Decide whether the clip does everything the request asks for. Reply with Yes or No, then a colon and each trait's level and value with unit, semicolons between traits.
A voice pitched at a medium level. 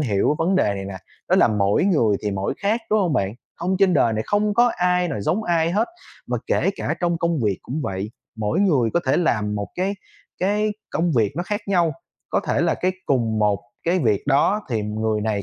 Yes: medium, 150 Hz